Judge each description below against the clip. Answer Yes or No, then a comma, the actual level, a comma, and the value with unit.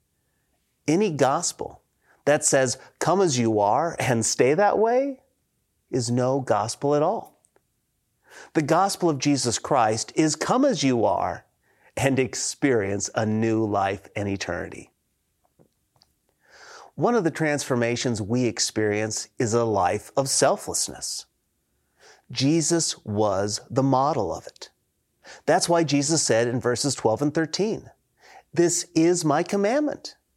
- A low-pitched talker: Yes, low, 130 Hz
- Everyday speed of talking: No, slow, 125 wpm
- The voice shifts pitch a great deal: Yes, wide, 6.5 semitones